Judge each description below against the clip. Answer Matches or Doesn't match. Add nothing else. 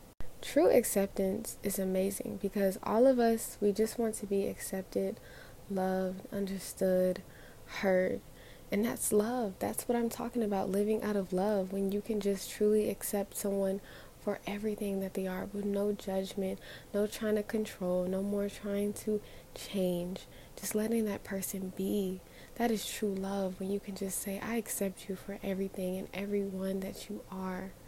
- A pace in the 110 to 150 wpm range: Doesn't match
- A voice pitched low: Doesn't match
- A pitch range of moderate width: Doesn't match